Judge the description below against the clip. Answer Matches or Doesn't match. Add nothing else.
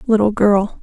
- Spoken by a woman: Matches